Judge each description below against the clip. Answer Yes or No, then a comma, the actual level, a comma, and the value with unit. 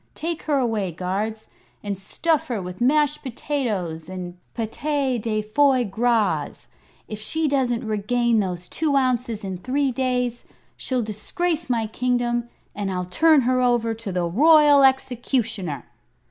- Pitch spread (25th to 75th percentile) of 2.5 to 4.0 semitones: No, average, 4.5 semitones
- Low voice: No, high, 240 Hz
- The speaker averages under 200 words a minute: Yes, average, 140 wpm